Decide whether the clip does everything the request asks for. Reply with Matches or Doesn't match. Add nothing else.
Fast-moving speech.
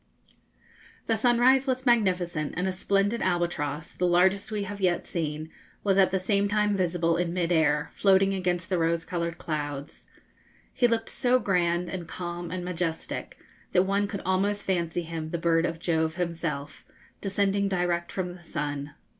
Doesn't match